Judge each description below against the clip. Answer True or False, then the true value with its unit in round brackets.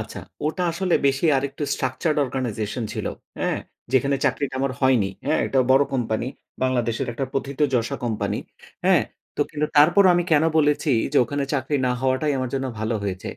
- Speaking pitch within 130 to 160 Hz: True (135 Hz)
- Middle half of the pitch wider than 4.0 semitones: False (3.0 semitones)